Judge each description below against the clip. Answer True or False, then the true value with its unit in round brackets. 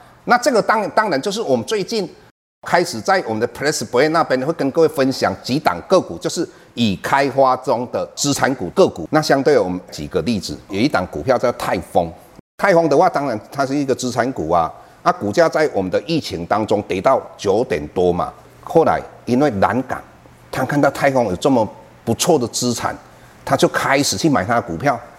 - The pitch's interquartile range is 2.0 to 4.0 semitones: True (2.6 semitones)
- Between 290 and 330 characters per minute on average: True (305 characters per minute)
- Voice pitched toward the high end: False (130 Hz)